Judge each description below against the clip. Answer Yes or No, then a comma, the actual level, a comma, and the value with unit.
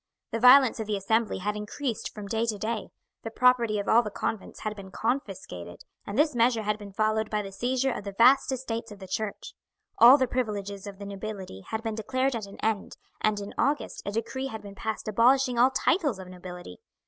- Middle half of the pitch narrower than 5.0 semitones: Yes, average, 3.4 semitones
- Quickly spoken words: Yes, fast, 215 wpm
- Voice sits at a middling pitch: No, high, 220 Hz